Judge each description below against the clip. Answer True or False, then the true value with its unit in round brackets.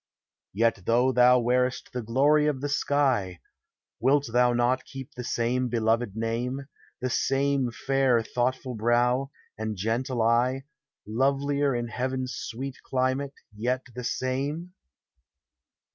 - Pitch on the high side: False (125 Hz)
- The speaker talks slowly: True (125 wpm)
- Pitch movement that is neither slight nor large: False (2.2 semitones)